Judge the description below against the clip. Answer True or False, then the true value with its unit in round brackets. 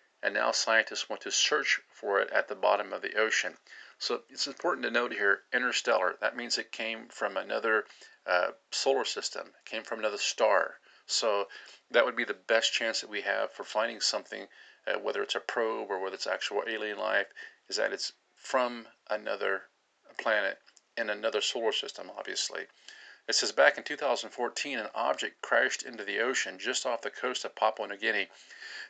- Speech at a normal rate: True (185 wpm)